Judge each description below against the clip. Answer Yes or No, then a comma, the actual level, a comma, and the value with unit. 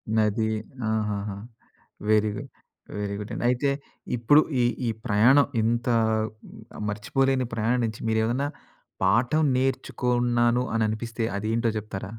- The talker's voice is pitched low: Yes, low, 115 Hz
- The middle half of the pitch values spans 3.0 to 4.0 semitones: No, narrow, 2.5 semitones